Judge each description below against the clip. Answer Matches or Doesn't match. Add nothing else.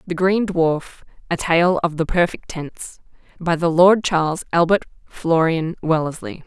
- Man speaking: Doesn't match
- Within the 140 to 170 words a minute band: Matches